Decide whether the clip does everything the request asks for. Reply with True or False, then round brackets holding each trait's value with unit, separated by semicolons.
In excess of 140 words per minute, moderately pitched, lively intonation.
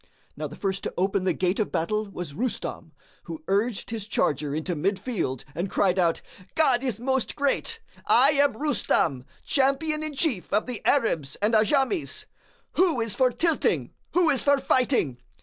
False (170 wpm; 225 Hz; 6.9 semitones)